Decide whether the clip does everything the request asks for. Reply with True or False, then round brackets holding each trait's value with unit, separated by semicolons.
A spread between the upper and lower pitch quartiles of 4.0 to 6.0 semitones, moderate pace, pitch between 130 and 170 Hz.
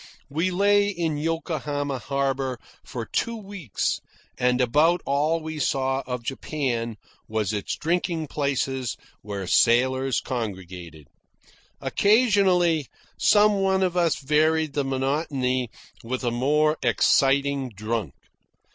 False (4.7 semitones; 110 wpm; 140 Hz)